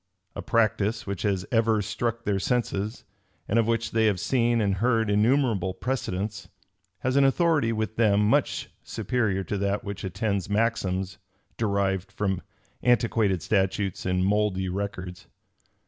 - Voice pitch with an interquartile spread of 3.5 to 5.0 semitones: No, average, 3.0 semitones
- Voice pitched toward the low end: Yes, low, 105 Hz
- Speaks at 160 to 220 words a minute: No, average, 140 wpm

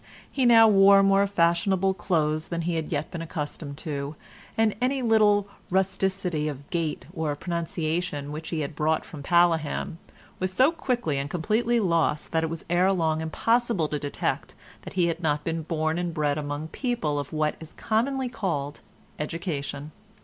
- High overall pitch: No, medium, 165 Hz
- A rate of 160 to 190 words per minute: Yes, average, 170 wpm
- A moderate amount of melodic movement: Yes, average, 4.2 semitones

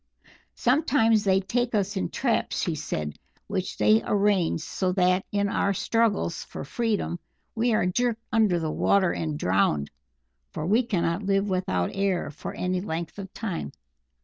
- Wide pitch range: No, average, 4.4 semitones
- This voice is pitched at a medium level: No, high, 195 Hz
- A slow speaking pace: No, average, 155 wpm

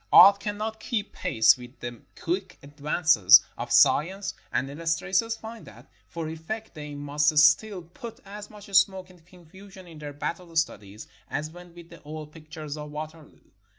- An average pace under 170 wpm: Yes, average, 160 wpm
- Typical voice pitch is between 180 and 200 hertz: No, medium, 165 Hz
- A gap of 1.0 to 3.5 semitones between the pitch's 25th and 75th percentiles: No, average, 4.4 semitones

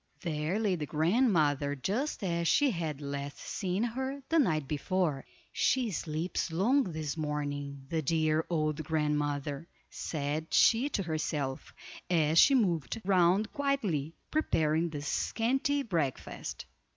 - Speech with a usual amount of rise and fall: No, wide, 5.8 semitones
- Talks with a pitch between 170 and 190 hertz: No, medium, 160 Hz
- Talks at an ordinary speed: No, slow, 125 wpm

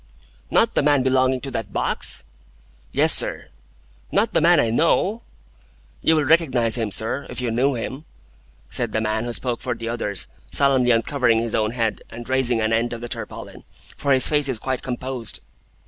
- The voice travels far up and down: No, narrow, 2.6 semitones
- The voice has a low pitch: Yes, low, 125 Hz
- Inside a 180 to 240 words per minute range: Yes, average, 185 wpm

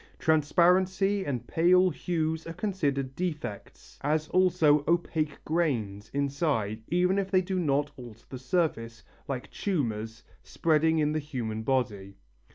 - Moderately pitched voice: Yes, medium, 155 Hz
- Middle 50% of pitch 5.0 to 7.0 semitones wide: Yes, wide, 5.5 semitones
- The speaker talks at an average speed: No, slow, 130 wpm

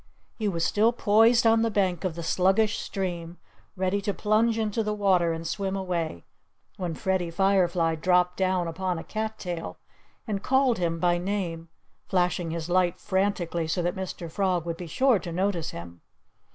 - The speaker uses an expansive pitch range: No, average, 3.1 semitones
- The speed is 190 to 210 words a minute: No, average, 175 wpm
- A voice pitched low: No, medium, 185 Hz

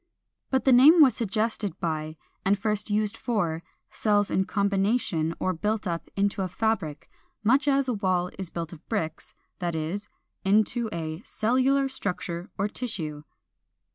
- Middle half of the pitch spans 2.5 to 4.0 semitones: No, average, 4.7 semitones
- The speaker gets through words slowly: No, average, 160 wpm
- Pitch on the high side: Yes, high, 205 Hz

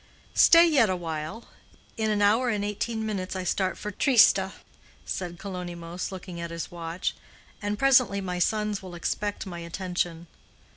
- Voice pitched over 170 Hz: Yes, high, 190 Hz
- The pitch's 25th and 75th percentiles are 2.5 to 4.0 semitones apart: Yes, average, 3.5 semitones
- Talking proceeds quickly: No, average, 155 wpm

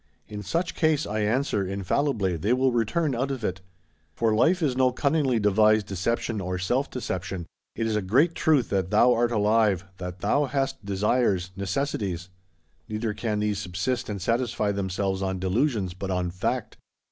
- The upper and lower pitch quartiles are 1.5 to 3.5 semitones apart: No, average, 4.8 semitones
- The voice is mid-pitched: No, low, 105 Hz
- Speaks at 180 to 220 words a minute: No, average, 170 wpm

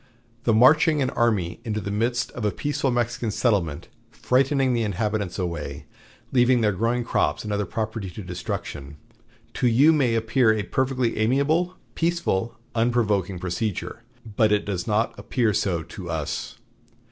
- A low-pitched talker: Yes, low, 110 Hz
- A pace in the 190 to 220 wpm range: No, average, 150 wpm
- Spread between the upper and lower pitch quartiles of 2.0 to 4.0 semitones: Yes, average, 3.7 semitones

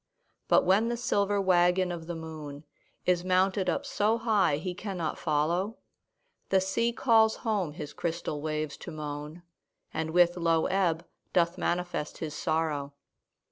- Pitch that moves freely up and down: No, average, 3.4 semitones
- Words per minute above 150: No, average, 145 wpm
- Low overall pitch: No, medium, 175 Hz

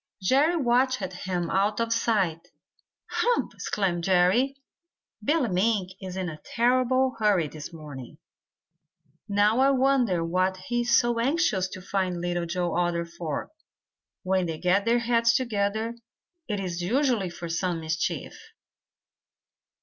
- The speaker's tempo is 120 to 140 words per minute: Yes, slow, 135 wpm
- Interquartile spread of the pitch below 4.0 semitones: No, average, 5.2 semitones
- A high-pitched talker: Yes, high, 195 Hz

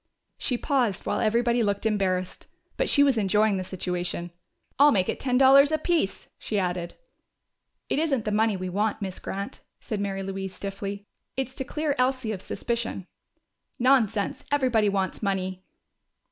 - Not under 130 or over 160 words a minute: Yes, average, 155 wpm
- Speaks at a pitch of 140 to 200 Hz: No, high, 210 Hz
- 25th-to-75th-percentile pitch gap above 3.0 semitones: Yes, average, 4.8 semitones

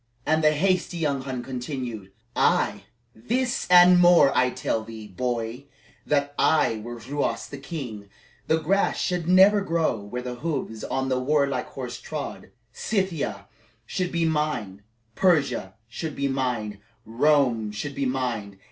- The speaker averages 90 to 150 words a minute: Yes, average, 145 wpm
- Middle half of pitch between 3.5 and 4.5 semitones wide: No, average, 5.3 semitones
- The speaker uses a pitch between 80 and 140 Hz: Yes, low, 135 Hz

